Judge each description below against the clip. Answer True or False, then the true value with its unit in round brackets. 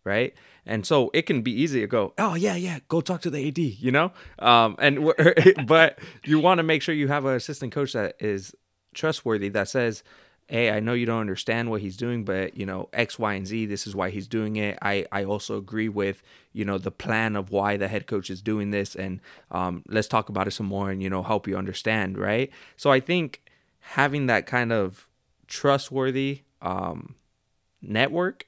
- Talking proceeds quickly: True (215 wpm)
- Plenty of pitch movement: True (6.1 semitones)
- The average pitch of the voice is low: True (110 Hz)